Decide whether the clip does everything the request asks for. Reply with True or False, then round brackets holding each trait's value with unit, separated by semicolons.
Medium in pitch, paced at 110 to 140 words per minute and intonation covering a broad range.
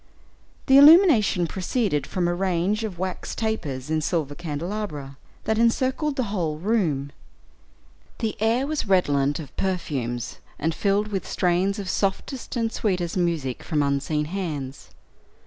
True (180 Hz; 135 wpm; 6.1 semitones)